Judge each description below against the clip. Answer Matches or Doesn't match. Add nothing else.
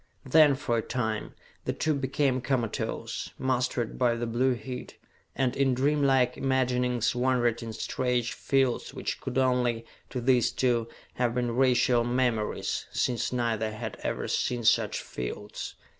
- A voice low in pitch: Matches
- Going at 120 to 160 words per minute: Matches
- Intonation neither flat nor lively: Doesn't match